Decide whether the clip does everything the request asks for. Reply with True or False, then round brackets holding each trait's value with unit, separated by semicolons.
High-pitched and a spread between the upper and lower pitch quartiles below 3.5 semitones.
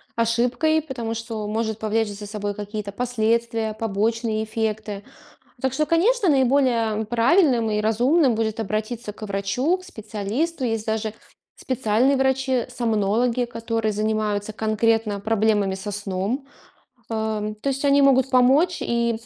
True (225 Hz; 3.1 semitones)